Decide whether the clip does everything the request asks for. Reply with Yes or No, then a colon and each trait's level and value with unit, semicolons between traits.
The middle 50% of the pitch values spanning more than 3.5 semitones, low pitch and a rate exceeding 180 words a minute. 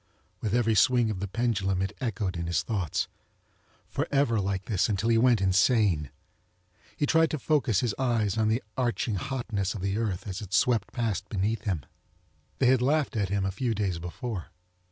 Yes: average, 3.9 semitones; low, 110 Hz; average, 190 wpm